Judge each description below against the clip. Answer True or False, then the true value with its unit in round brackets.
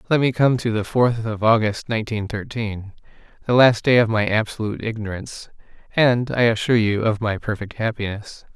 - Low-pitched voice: True (110 Hz)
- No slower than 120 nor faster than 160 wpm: False (170 wpm)